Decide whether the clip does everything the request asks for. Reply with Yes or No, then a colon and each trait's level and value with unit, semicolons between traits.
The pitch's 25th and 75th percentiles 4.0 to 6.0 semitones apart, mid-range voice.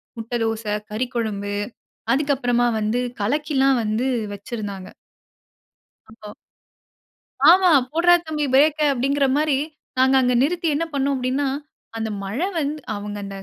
No: average, 4.9 semitones; very high, 255 Hz